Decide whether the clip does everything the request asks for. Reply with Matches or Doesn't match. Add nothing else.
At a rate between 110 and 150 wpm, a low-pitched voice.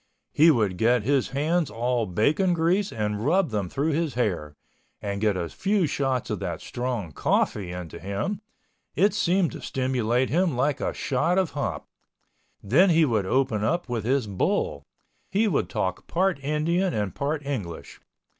Doesn't match